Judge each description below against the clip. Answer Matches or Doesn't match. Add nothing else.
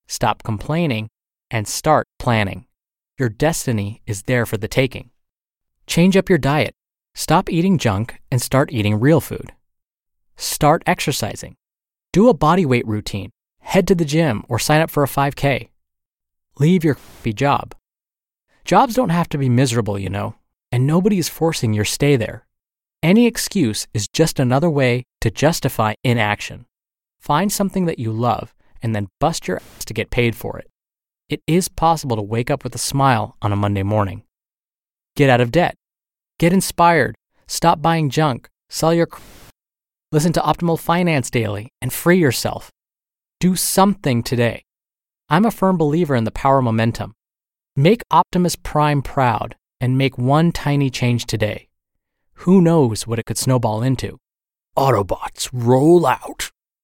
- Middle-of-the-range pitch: Doesn't match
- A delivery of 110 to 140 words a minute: Doesn't match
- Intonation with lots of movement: Matches